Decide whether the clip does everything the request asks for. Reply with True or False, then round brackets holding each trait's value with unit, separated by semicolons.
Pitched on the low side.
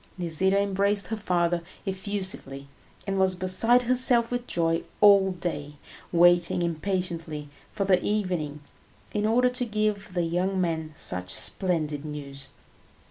False (185 Hz)